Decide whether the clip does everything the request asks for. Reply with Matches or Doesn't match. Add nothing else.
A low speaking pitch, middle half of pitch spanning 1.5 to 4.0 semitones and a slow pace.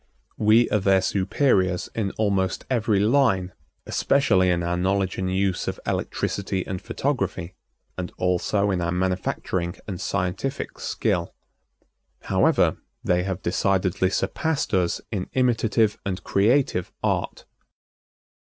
Matches